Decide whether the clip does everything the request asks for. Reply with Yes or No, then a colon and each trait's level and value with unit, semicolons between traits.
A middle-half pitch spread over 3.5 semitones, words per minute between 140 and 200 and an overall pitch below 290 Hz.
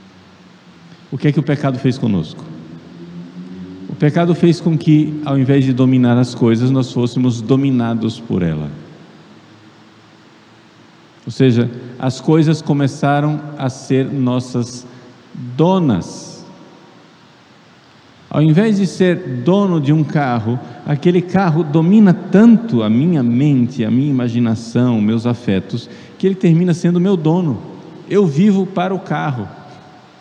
No: wide, 5.6 semitones; average, 125 wpm; low, 135 Hz